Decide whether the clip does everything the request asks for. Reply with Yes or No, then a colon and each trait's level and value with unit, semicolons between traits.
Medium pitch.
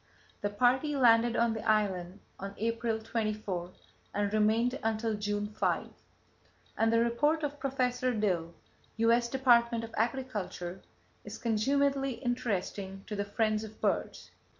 No: high, 225 Hz